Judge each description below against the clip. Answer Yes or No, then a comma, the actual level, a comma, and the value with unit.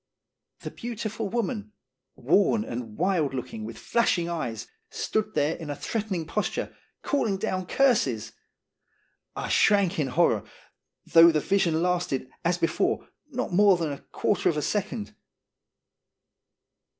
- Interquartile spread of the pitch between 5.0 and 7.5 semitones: Yes, wide, 5.6 semitones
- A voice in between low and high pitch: Yes, medium, 180 Hz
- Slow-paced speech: Yes, slow, 130 wpm